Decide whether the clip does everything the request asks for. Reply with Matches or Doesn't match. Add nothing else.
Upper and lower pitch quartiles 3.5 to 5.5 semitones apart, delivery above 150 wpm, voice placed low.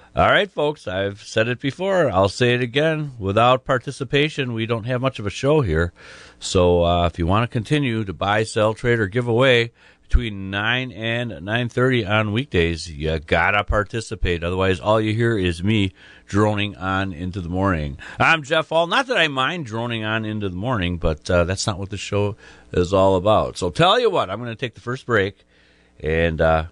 Matches